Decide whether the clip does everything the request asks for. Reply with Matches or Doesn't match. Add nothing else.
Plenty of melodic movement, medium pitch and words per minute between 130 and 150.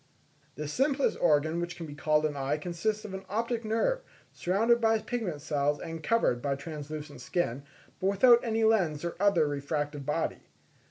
Doesn't match